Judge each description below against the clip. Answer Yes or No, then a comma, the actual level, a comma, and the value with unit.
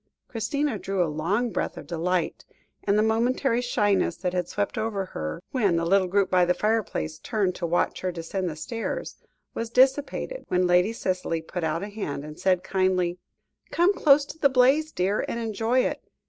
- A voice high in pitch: Yes, high, 195 Hz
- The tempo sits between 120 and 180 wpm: No, average, 190 wpm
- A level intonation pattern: No, average, 4.6 semitones